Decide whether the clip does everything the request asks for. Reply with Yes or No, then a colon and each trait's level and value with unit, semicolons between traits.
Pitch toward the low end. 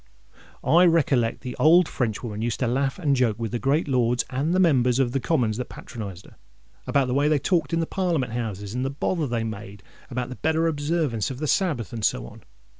Yes: low, 130 Hz